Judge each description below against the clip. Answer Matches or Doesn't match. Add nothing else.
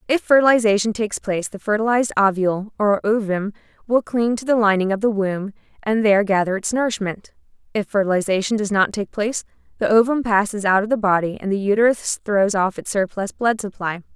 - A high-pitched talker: Matches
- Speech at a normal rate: Matches